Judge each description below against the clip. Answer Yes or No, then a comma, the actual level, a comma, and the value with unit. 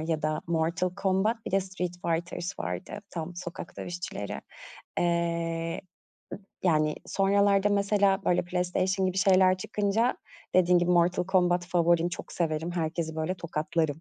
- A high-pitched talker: No, medium, 175 Hz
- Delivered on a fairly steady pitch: Yes, narrow, 2.2 semitones